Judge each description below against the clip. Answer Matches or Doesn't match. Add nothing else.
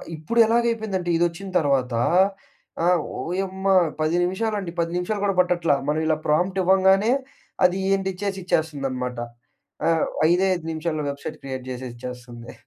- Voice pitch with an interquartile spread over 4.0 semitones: Matches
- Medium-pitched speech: Matches